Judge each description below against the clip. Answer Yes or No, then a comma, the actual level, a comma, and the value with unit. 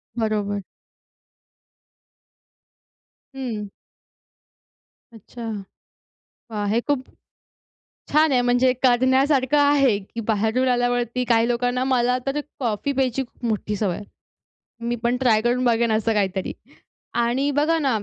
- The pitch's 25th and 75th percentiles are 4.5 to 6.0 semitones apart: No, average, 2.8 semitones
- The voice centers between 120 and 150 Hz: No, high, 245 Hz